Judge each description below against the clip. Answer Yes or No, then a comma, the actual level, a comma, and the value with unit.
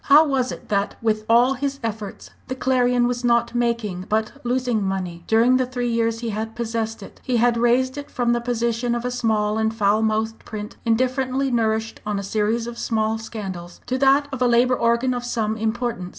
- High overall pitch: Yes, high, 235 Hz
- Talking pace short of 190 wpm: No, fast, 205 wpm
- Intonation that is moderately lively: No, narrow, 2.1 semitones